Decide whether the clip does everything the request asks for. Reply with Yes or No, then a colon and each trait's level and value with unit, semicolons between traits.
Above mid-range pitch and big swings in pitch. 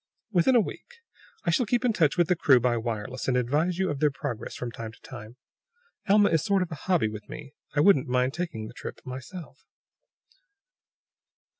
No: medium, 145 Hz; wide, 6.5 semitones